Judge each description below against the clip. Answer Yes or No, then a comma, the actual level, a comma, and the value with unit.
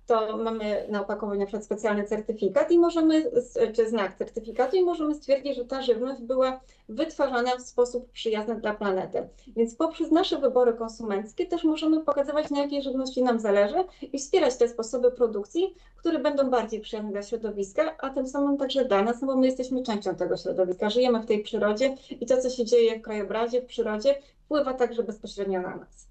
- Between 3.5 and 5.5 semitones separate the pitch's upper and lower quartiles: Yes, average, 4.5 semitones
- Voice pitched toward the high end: Yes, high, 245 Hz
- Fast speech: Yes, fast, 180 wpm